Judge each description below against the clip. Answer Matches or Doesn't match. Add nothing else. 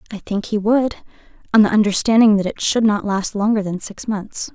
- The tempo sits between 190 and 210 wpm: Matches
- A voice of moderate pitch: Doesn't match